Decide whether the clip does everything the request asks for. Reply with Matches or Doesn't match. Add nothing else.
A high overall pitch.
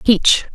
Matches